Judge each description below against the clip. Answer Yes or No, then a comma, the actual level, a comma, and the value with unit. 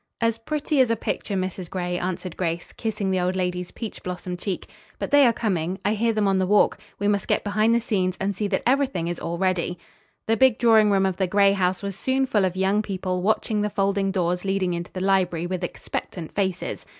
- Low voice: No, high, 195 Hz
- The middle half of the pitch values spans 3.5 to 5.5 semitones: No, average, 2.7 semitones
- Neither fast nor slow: No, fast, 225 wpm